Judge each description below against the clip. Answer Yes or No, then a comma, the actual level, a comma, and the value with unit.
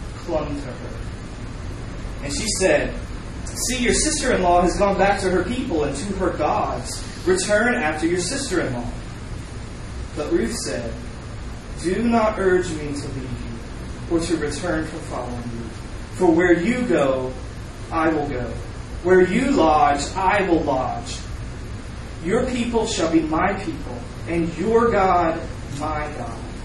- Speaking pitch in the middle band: Yes, medium, 160 Hz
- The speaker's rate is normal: Yes, average, 150 wpm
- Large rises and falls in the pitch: Yes, wide, 7.2 semitones